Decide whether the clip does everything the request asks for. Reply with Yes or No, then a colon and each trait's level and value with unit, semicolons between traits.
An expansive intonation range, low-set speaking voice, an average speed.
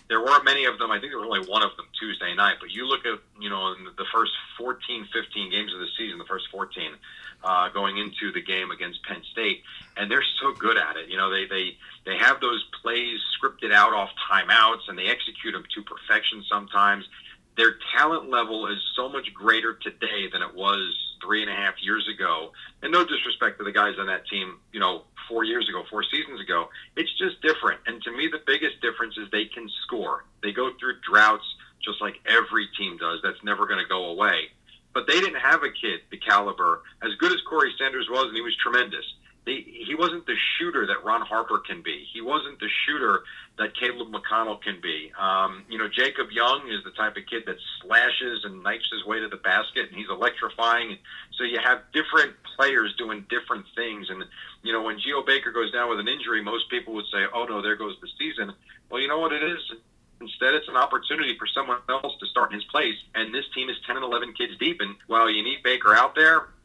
No: wide, 7.2 semitones; low, 115 Hz; fast, 225 wpm